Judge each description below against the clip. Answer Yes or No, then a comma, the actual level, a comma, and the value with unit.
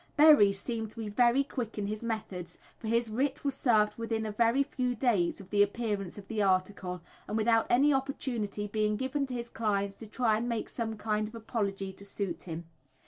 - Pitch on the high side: Yes, high, 220 Hz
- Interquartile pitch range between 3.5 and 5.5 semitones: No, average, 2.8 semitones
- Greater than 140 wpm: Yes, fast, 205 wpm